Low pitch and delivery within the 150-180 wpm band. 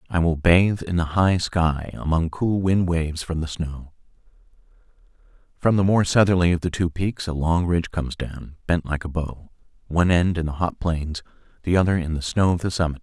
No: very low, 85 Hz; fast, 205 wpm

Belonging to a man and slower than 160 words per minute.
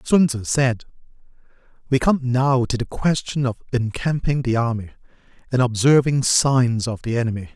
Yes: male; average, 150 wpm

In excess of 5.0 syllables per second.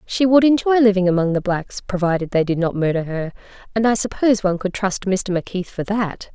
Yes: 5.9 syllables/s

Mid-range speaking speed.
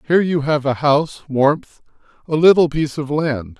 Yes: average, 185 wpm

